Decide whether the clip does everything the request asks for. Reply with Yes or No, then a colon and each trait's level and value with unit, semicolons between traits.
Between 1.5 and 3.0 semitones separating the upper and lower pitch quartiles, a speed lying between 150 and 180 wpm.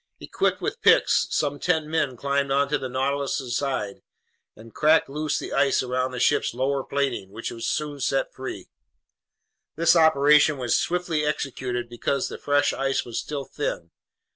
Yes: average, 2.7 semitones; average, 160 wpm